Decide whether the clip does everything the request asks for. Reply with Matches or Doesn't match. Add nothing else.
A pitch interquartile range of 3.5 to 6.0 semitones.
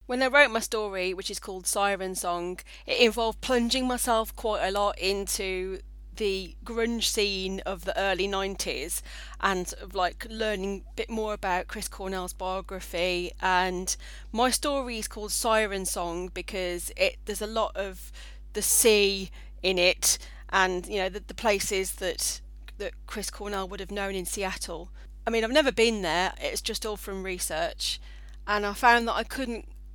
Doesn't match